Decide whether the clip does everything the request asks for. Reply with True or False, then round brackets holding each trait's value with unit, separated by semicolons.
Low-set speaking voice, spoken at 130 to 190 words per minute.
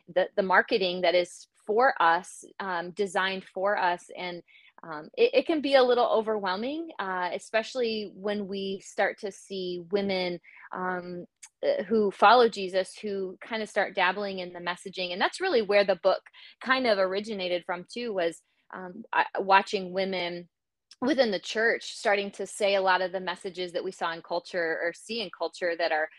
False (190 Hz; 175 wpm)